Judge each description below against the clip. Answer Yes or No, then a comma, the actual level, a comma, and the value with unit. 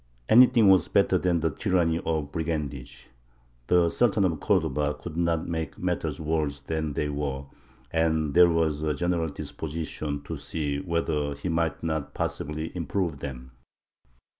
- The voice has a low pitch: Yes, very low, 80 Hz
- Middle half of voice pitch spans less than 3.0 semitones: Yes, narrow, 2.4 semitones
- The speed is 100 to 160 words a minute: Yes, average, 145 wpm